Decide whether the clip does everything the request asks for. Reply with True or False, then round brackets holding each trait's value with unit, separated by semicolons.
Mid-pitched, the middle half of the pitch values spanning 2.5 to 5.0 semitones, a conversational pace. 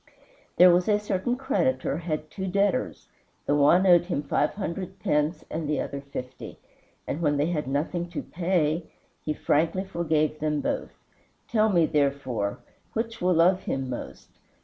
True (165 Hz; 4.0 semitones; 160 wpm)